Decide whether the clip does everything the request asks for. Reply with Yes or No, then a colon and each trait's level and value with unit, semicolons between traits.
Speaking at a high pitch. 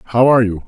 No: low, 115 Hz